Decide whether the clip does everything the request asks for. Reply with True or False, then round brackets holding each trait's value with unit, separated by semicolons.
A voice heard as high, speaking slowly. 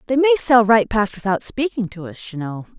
False (220 Hz; 235 wpm)